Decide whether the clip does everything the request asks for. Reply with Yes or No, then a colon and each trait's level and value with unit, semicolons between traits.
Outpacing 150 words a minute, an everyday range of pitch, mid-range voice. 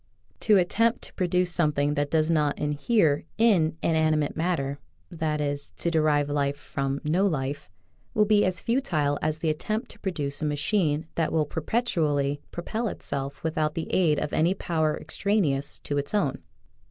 Yes: average, 170 wpm; average, 3.7 semitones; medium, 155 Hz